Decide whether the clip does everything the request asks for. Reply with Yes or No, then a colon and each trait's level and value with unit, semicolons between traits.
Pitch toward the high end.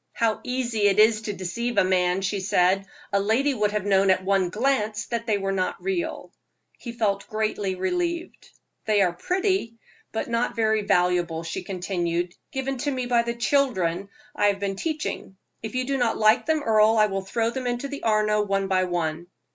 Yes: high, 215 Hz